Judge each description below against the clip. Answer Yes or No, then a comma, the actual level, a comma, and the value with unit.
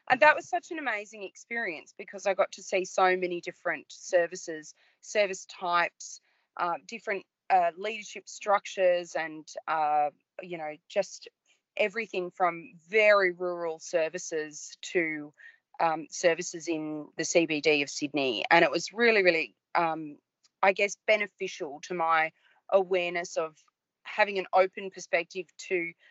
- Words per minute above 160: No, slow, 135 wpm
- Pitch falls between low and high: Yes, medium, 180 Hz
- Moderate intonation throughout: Yes, average, 3.6 semitones